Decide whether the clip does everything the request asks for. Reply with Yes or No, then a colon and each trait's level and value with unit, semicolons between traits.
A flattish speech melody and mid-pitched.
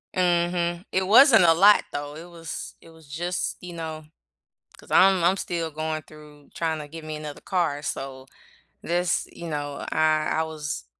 Yes: narrow, 2.3 semitones; medium, 160 Hz